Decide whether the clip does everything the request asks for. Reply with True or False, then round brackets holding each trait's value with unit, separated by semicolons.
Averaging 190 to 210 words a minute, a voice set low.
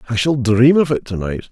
False (275 wpm; 125 Hz)